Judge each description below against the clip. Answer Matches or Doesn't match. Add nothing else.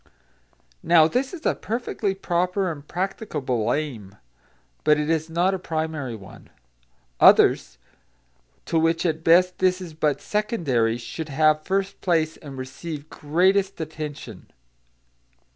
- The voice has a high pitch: Doesn't match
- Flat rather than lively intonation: Doesn't match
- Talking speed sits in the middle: Doesn't match